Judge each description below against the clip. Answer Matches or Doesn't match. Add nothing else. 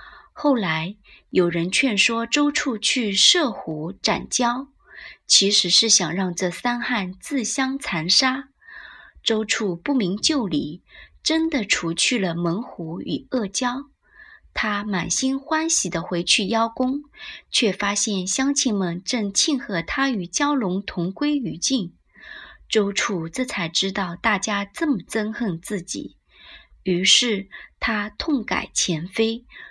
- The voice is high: Matches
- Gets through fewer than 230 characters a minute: Matches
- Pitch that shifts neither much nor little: Doesn't match